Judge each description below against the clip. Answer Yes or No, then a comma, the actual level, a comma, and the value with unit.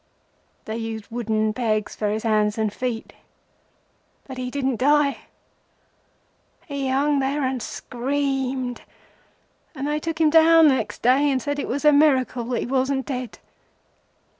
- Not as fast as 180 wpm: Yes, average, 150 wpm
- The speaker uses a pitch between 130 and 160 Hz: No, very high, 260 Hz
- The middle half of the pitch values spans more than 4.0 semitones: No, average, 3.5 semitones